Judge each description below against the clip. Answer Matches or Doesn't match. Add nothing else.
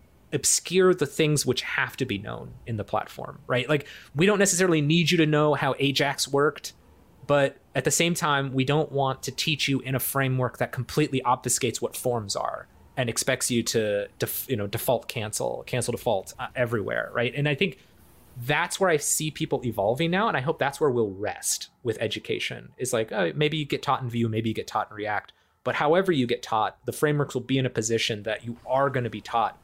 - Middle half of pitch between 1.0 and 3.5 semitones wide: Doesn't match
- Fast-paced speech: Matches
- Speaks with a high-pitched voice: Doesn't match